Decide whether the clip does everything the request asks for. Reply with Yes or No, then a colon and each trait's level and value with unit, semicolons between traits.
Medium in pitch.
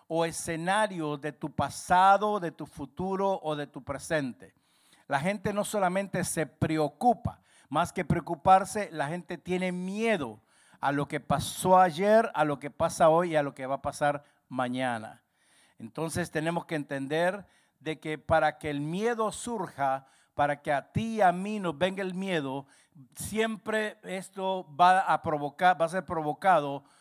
Yes: medium, 165 Hz